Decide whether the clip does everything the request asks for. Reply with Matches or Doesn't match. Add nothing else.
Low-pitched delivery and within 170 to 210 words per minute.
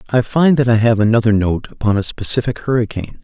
Matches